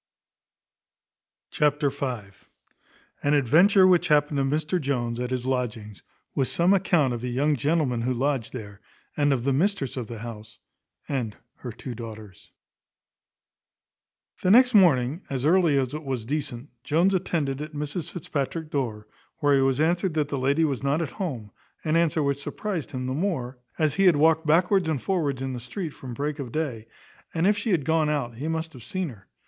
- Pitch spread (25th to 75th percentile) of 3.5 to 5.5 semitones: Yes, average, 4.3 semitones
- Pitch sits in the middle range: Yes, medium, 145 Hz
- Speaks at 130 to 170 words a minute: No, average, 185 wpm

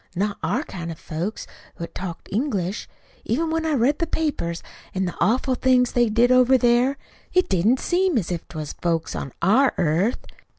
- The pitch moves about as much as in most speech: No, wide, 6.9 semitones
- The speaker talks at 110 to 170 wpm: No, average, 185 wpm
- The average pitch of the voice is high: Yes, high, 235 Hz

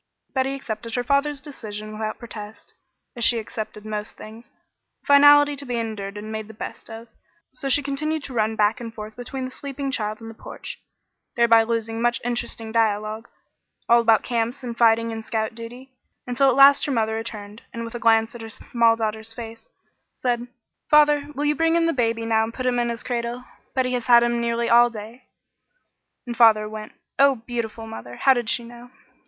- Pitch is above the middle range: Yes, high, 230 Hz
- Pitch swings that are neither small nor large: No, narrow, 2.2 semitones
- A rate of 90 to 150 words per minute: No, average, 195 wpm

